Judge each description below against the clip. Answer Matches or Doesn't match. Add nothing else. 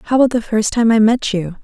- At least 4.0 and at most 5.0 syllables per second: Doesn't match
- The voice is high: Matches